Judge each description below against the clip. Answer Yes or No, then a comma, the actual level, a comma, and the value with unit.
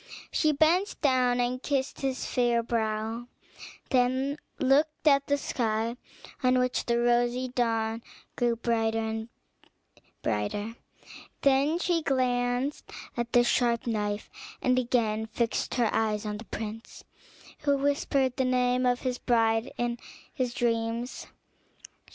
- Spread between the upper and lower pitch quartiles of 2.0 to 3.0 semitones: Yes, narrow, 2.5 semitones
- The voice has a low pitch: No, high, 245 Hz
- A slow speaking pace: Yes, slow, 125 wpm